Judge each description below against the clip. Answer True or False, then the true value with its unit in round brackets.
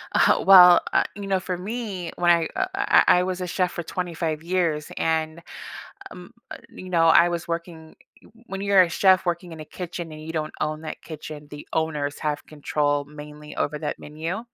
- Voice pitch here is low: False (170 Hz)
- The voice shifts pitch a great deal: False (2.9 semitones)